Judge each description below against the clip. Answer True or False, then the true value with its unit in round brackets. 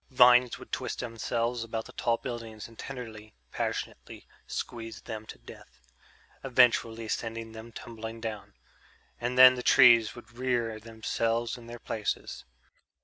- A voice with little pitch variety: True (1.4 semitones)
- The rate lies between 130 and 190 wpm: True (140 wpm)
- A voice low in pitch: True (115 Hz)